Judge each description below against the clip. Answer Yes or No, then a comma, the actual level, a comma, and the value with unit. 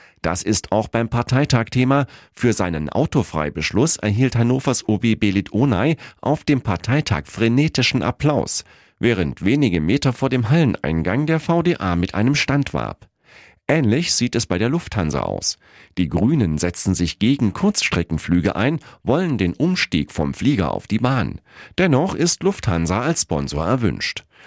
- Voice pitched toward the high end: No, low, 120 Hz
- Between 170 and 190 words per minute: No, average, 140 wpm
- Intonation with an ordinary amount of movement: No, wide, 7.4 semitones